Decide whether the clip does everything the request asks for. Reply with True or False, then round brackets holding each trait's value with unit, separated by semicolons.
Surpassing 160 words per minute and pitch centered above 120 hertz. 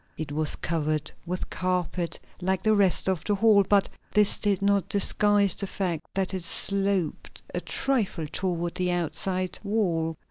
False (155 wpm; 185 Hz)